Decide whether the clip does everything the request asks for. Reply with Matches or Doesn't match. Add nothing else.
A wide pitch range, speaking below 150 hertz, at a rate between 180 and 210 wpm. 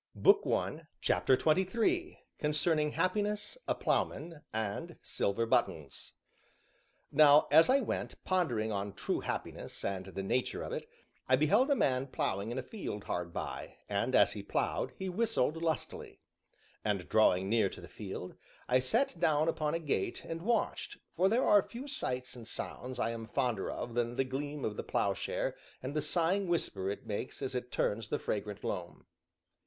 Doesn't match